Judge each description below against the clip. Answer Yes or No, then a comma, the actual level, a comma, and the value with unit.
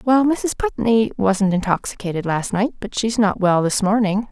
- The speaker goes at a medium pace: Yes, average, 180 wpm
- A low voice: No, high, 210 Hz